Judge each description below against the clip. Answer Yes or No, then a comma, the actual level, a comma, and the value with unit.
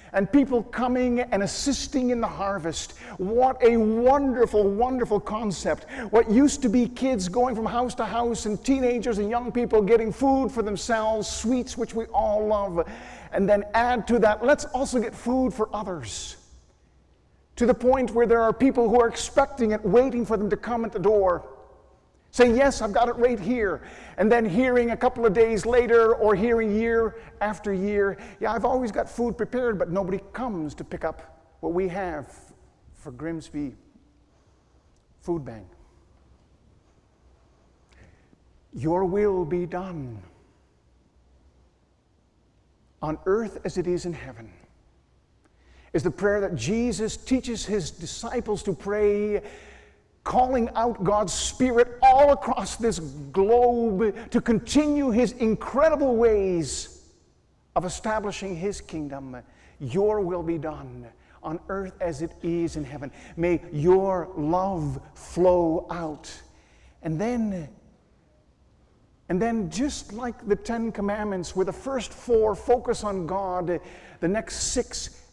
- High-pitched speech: Yes, high, 210 Hz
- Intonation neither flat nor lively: No, wide, 5.7 semitones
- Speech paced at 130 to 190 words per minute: Yes, average, 145 wpm